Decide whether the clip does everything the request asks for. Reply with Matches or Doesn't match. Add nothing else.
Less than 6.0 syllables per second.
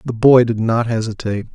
Matches